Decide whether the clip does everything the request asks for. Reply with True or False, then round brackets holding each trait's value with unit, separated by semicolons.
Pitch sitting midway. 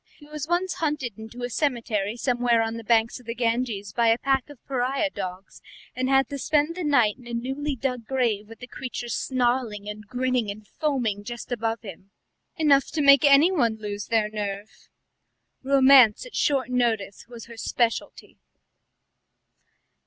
False (240 Hz)